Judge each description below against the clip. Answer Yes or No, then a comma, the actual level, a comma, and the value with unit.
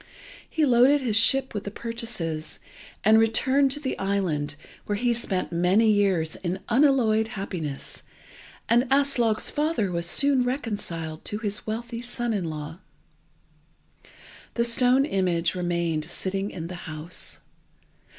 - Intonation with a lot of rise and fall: Yes, wide, 5.7 semitones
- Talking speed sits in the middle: No, slow, 130 wpm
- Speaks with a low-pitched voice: No, high, 215 Hz